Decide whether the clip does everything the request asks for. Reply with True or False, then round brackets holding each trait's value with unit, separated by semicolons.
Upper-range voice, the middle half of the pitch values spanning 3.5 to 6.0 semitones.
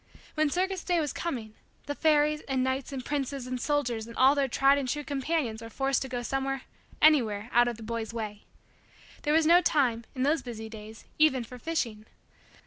True (265 Hz; 4.2 semitones)